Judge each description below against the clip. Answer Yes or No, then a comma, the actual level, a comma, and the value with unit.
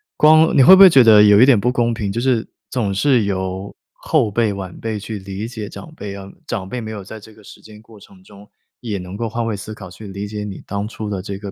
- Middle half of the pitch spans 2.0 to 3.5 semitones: Yes, average, 2.8 semitones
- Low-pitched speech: Yes, low, 105 Hz